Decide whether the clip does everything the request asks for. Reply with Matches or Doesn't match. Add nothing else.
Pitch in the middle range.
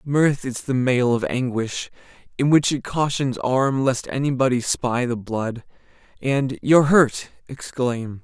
Doesn't match